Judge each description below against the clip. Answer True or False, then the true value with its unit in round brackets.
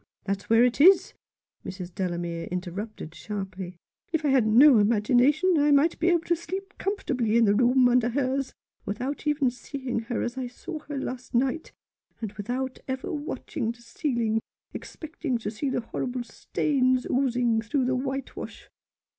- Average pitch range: True (4.2 semitones)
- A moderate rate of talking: True (165 wpm)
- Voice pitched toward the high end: True (250 Hz)